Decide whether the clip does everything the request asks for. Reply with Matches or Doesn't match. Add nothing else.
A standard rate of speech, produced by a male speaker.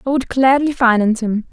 Doesn't match